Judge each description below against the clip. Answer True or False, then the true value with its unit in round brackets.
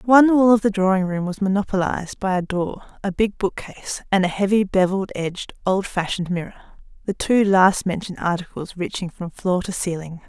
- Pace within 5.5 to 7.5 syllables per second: True (5.8 syllables/s)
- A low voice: False (190 Hz)